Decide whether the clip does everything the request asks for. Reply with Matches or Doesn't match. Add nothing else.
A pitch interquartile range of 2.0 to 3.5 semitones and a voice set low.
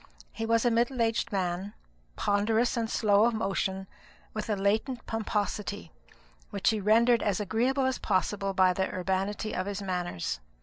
Doesn't match